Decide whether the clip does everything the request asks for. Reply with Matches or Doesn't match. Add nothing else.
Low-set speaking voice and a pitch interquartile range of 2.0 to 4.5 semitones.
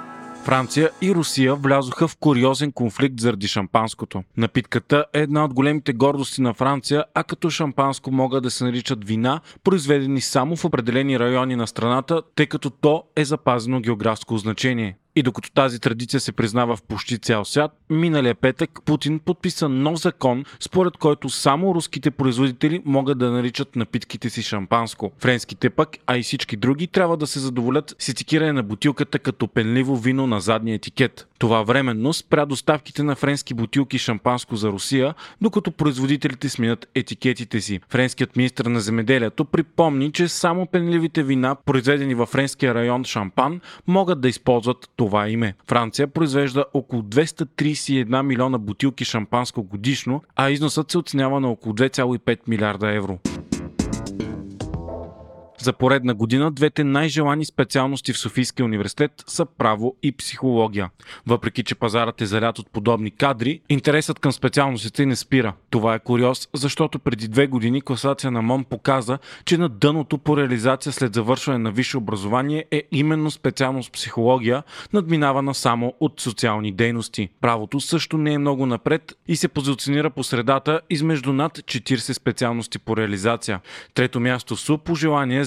Matches